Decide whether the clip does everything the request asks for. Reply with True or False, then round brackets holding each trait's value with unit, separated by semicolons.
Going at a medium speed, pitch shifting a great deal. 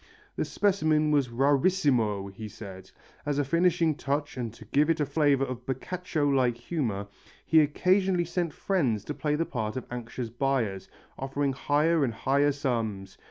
False (160 wpm; 4.7 semitones)